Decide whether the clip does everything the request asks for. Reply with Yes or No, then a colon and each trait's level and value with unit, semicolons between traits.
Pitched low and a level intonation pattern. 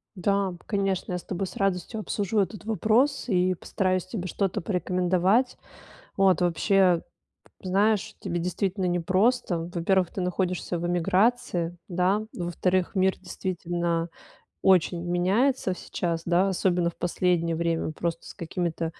No: medium, 185 Hz; narrow, 2.1 semitones